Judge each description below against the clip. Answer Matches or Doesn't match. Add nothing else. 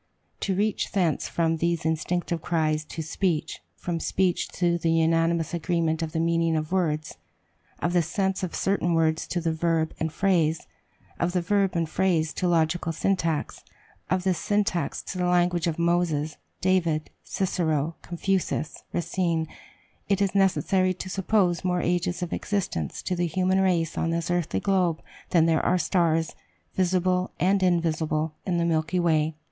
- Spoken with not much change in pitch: Matches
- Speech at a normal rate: Matches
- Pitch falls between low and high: Matches